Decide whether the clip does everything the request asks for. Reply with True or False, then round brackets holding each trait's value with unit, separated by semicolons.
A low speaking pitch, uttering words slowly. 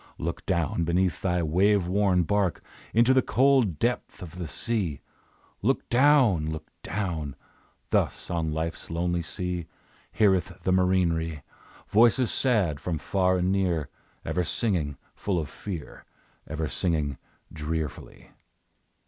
True (90 Hz; 125 wpm)